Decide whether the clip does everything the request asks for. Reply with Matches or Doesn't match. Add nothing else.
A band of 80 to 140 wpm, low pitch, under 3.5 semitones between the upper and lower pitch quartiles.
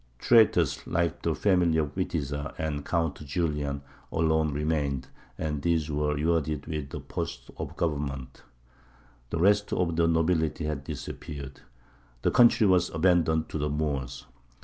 Matches